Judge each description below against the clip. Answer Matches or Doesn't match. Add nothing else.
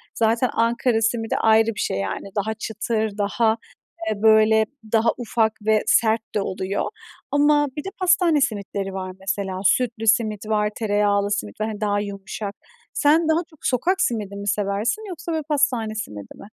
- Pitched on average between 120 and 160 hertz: Doesn't match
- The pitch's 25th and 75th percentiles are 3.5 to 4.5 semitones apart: Doesn't match